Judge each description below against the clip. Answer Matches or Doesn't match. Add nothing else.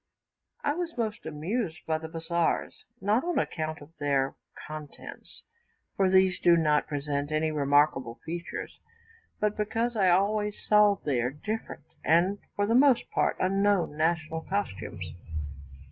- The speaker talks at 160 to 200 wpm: Doesn't match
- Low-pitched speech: Doesn't match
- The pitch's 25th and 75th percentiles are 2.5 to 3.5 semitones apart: Doesn't match